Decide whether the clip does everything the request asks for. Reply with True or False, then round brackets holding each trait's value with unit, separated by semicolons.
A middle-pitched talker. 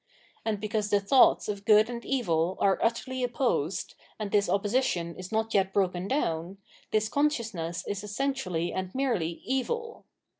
False (210 Hz)